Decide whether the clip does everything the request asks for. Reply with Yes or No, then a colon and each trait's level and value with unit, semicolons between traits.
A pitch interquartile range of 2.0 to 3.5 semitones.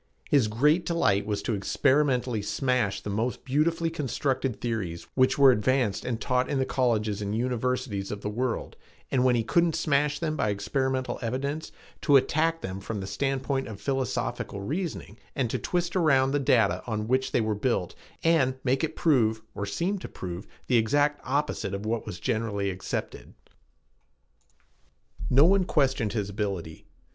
No: average, 5.1 semitones